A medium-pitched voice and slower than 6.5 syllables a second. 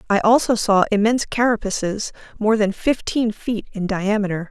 No: high, 215 Hz; 5.1 syllables/s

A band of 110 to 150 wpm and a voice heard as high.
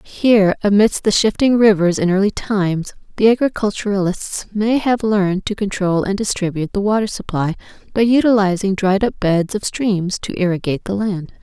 No: average, 165 wpm; high, 200 Hz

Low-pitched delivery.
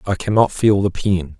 Yes: very low, 95 Hz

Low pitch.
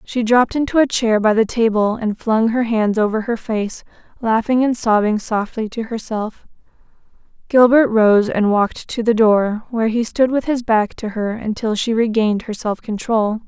No: high, 225 Hz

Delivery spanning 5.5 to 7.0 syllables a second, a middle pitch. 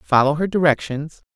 No: 5.0 syllables/s; medium, 155 Hz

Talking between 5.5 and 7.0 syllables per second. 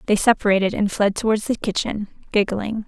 Yes: 5.7 syllables/s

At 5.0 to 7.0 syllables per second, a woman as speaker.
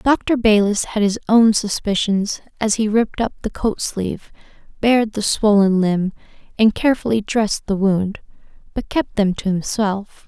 No: 4.6 syllables/s; female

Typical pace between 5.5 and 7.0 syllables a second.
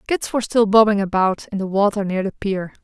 Yes: 5.8 syllables/s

